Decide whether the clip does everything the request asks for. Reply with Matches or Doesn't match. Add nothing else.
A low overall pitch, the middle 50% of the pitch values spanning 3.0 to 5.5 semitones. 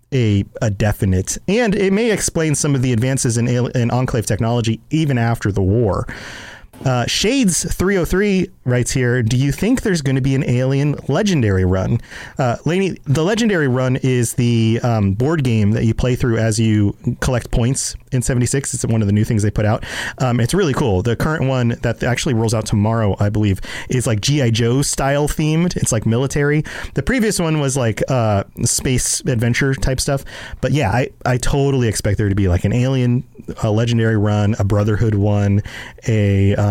Matches